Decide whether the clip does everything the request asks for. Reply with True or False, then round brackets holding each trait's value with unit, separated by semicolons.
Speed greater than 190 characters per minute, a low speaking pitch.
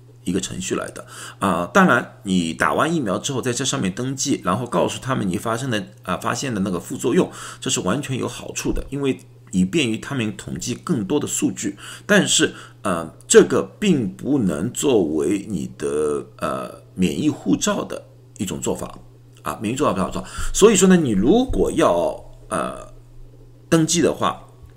True (260 characters per minute; 125 Hz)